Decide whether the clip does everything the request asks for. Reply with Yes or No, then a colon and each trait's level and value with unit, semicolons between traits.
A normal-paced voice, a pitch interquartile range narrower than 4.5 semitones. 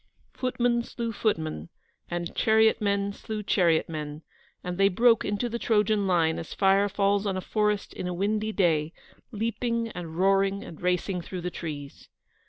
Yes: average, 165 wpm; average, 3.8 semitones